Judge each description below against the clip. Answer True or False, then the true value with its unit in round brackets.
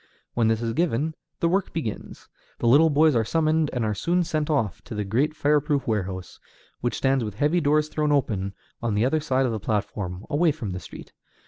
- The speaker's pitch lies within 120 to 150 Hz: True (135 Hz)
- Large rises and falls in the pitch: True (6.0 semitones)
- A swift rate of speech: True (215 wpm)